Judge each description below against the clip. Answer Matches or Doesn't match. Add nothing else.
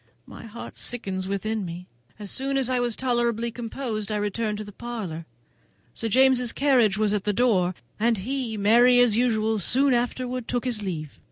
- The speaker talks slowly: Doesn't match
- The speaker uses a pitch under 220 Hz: Doesn't match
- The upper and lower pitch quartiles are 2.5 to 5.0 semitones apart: Matches